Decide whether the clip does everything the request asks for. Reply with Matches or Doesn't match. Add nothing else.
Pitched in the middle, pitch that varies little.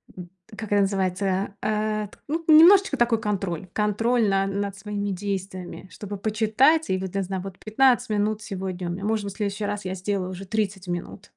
Doesn't match